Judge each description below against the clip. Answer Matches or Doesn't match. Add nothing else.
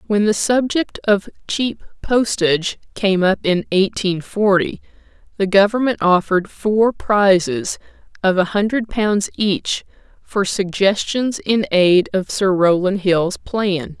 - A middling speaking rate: Doesn't match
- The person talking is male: Doesn't match